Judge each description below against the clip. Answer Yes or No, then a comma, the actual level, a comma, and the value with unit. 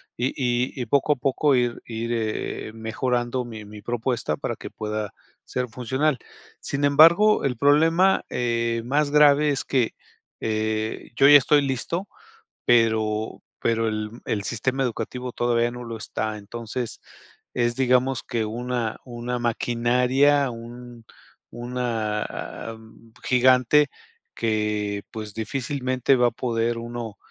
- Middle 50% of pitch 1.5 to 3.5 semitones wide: Yes, narrow, 2.6 semitones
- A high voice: No, low, 120 Hz